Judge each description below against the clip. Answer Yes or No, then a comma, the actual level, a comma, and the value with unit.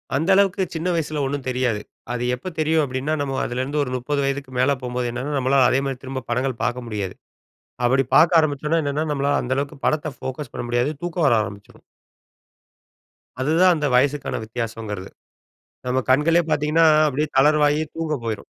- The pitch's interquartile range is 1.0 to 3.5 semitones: Yes, average, 3.2 semitones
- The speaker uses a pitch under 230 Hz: Yes, low, 135 Hz